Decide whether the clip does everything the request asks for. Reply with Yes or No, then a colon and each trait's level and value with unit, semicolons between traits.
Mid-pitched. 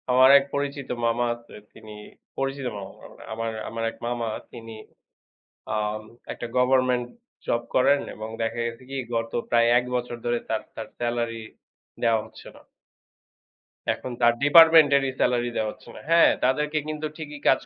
No: low, 120 Hz